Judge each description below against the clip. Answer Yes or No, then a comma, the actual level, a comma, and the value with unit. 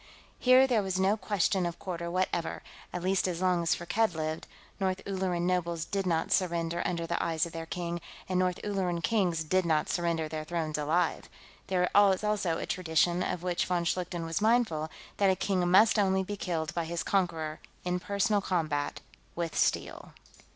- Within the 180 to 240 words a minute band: Yes, average, 185 wpm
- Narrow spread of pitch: Yes, narrow, 2.3 semitones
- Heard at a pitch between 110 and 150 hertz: No, medium, 180 Hz